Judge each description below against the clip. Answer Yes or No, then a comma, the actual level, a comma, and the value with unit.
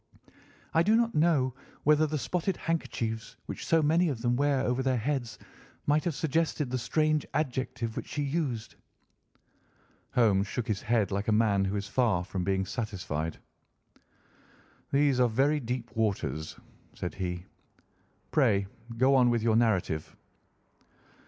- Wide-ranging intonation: Yes, wide, 5.7 semitones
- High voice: No, low, 125 Hz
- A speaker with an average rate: Yes, average, 145 wpm